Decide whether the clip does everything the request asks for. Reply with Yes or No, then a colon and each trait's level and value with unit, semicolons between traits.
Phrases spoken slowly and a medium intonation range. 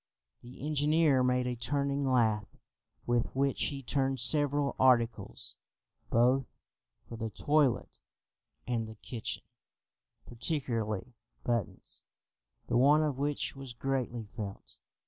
Yes: slow, 110 wpm; average, 3.0 semitones